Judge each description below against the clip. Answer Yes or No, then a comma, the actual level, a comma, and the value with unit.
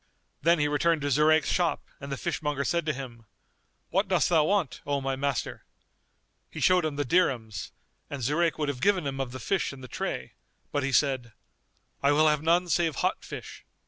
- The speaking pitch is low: No, medium, 145 Hz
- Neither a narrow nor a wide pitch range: Yes, average, 3.7 semitones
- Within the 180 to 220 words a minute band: Yes, average, 200 wpm